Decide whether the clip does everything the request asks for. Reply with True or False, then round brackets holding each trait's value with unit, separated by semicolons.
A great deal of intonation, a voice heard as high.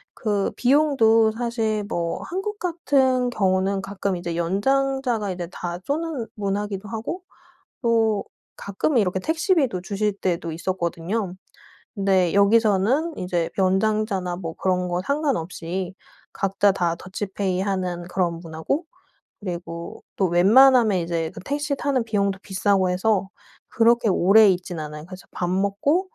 False (4.5 semitones; 200 Hz)